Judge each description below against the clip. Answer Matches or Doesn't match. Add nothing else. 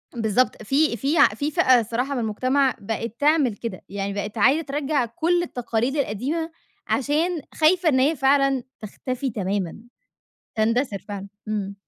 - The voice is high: Matches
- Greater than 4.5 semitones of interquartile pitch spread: Matches